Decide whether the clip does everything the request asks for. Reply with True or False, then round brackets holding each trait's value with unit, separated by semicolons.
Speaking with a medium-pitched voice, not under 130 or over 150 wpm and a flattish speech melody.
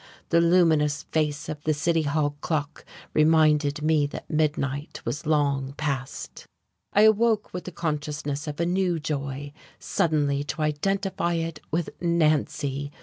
True (155 Hz; 140 wpm; 2.3 semitones)